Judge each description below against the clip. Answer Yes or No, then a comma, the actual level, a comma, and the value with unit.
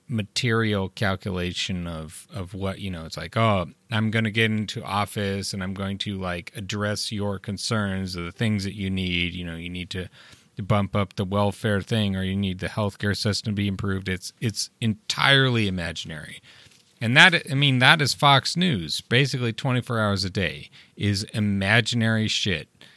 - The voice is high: No, low, 100 Hz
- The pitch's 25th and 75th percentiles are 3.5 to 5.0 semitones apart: No, average, 2.9 semitones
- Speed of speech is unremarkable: Yes, average, 185 wpm